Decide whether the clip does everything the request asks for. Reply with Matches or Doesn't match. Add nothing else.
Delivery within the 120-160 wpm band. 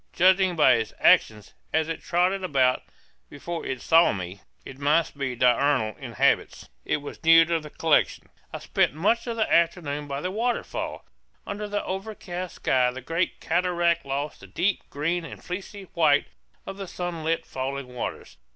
Doesn't match